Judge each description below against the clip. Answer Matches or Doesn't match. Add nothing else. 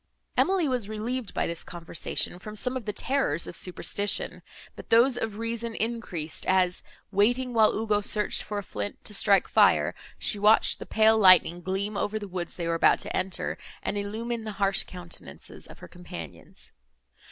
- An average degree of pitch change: Matches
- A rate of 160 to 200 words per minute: Matches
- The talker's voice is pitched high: Matches